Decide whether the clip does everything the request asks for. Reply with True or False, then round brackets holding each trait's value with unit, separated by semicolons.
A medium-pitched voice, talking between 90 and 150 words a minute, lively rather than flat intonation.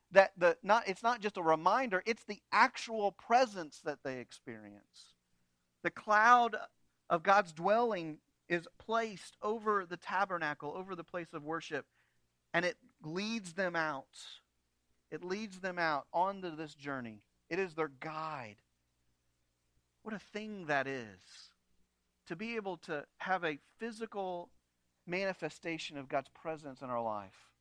True (165 Hz; 140 wpm; 9.0 semitones)